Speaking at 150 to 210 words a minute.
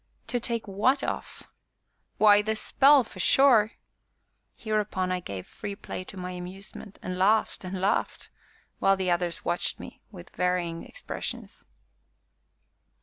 No: slow, 135 wpm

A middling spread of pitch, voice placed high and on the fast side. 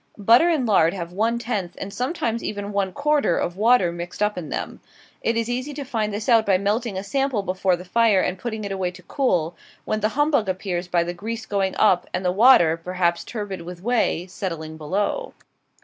Yes: average, 4.4 semitones; high, 200 Hz; fast, 210 wpm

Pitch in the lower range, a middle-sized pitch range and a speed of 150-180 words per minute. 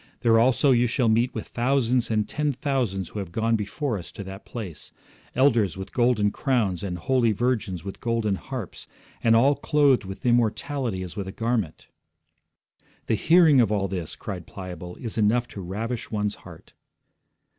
Yes: low, 115 Hz; average, 4.4 semitones; average, 170 wpm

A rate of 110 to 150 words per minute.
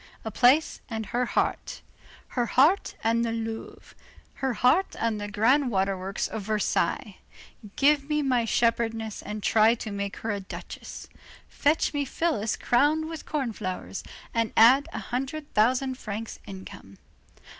Yes: average, 145 wpm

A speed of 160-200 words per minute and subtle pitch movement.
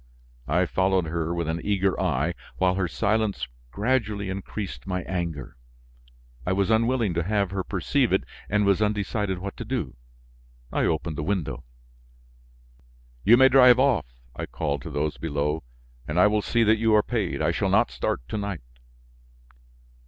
No: average, 165 wpm; average, 4.3 semitones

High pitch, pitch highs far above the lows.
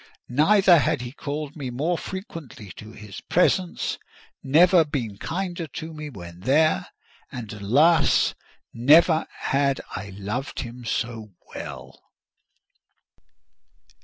No: medium, 140 Hz; wide, 6.3 semitones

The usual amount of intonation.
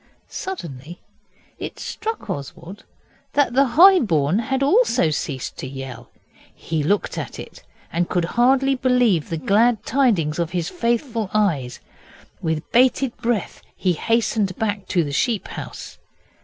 No: wide, 7.6 semitones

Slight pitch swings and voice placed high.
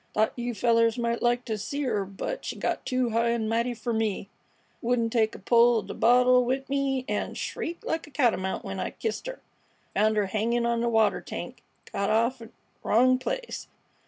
Yes: narrow, 2.3 semitones; high, 235 Hz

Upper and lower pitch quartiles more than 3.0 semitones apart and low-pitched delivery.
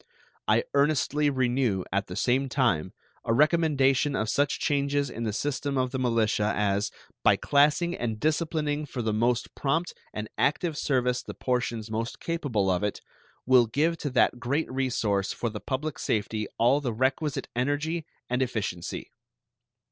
Yes: average, 4.4 semitones; low, 130 Hz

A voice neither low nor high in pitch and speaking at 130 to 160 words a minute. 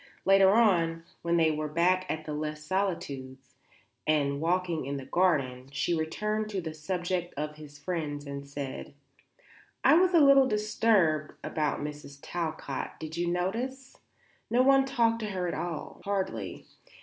Yes: medium, 170 Hz; average, 150 wpm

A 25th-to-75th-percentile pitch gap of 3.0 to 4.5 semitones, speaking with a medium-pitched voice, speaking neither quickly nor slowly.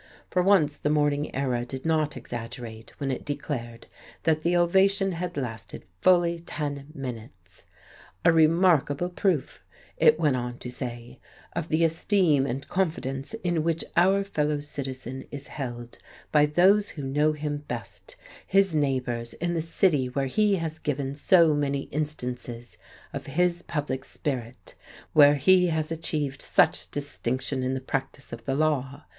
Yes: average, 4.1 semitones; medium, 145 Hz; average, 150 wpm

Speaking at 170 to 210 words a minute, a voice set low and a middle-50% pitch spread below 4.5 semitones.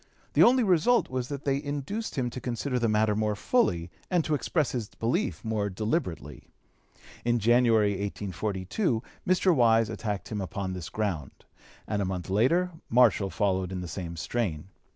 No: average, 175 wpm; low, 110 Hz; wide, 5.5 semitones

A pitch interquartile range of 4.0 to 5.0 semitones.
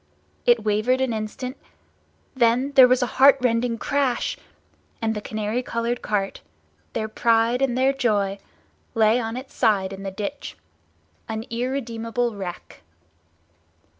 No: average, 2.9 semitones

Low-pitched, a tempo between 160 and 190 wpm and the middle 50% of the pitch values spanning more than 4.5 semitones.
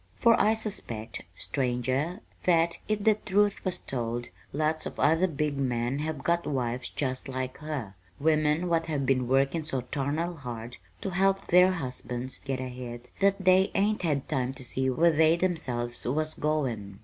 No: medium, 145 Hz; average, 165 wpm; average, 5.1 semitones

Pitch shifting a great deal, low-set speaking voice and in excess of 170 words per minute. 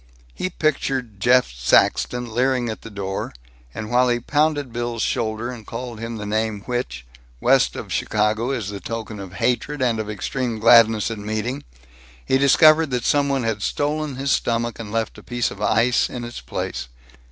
No: average, 2.9 semitones; low, 115 Hz; average, 180 wpm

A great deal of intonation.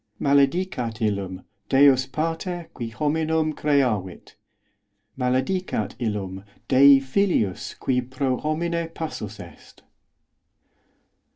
Yes: wide, 6.0 semitones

